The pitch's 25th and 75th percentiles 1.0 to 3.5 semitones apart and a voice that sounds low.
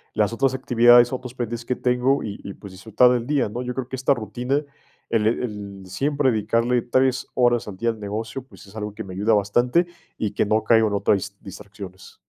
Yes: average, 3.2 semitones; low, 115 Hz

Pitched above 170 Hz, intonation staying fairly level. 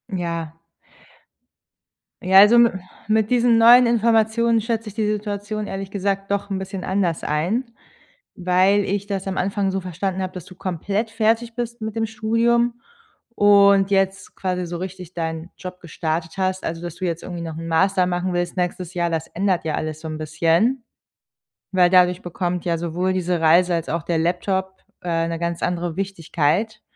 No: medium, 185 Hz; average, 3.2 semitones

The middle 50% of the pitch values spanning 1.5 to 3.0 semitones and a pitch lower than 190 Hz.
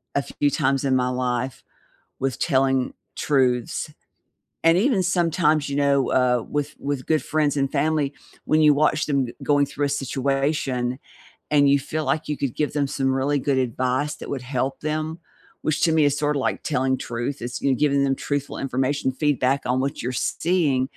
Yes: narrow, 2.4 semitones; medium, 140 Hz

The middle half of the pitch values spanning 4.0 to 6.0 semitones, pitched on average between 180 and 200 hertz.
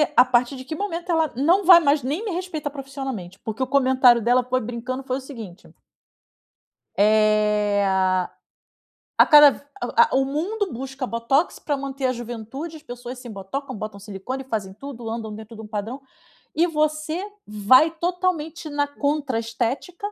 No: average, 5.1 semitones; very high, 260 Hz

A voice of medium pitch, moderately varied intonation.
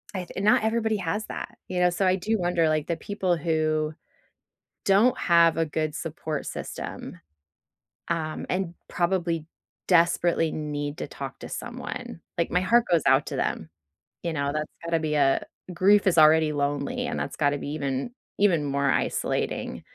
Yes: medium, 165 Hz; average, 3.3 semitones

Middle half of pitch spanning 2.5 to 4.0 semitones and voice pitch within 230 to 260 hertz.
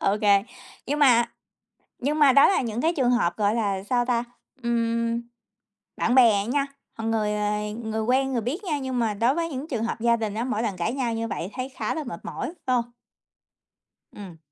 Yes: average, 3.4 semitones; high, 235 Hz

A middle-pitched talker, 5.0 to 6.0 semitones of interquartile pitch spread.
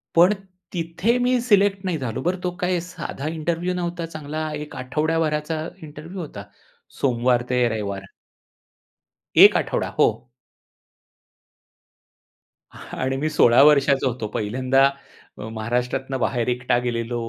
Yes: medium, 145 Hz; wide, 5.4 semitones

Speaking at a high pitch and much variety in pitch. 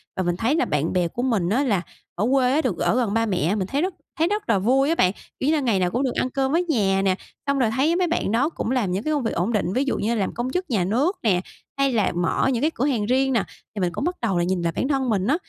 Yes: high, 235 Hz; wide, 6.2 semitones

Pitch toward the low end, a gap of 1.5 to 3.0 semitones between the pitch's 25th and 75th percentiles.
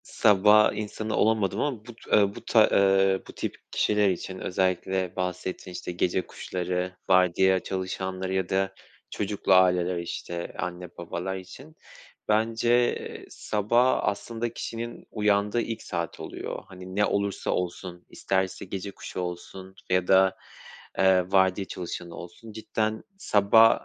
Yes: very low, 95 Hz; narrow, 2.5 semitones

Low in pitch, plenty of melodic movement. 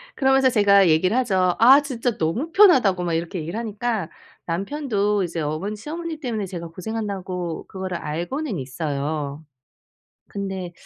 No: high, 195 Hz; wide, 6.1 semitones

